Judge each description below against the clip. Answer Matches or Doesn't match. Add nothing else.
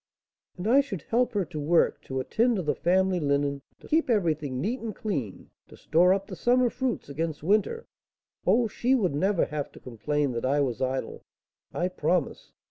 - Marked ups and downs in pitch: Matches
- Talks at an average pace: Matches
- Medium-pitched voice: Matches